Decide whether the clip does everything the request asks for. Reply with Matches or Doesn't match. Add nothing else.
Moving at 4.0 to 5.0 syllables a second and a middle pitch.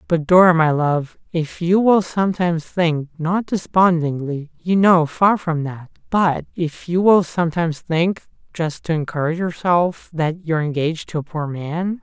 Matches